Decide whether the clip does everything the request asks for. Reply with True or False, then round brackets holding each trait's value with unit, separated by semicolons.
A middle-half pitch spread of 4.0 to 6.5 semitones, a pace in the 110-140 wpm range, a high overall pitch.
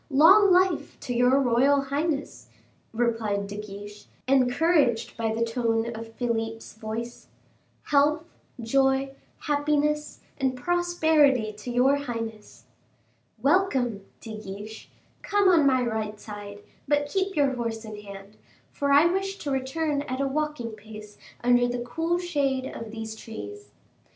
True (4.7 semitones; 135 wpm; 250 Hz)